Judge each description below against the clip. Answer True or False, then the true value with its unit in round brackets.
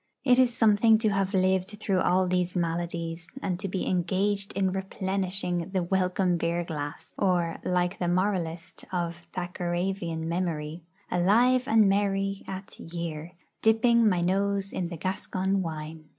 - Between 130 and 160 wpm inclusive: True (145 wpm)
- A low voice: False (185 Hz)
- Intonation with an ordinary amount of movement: False (2.3 semitones)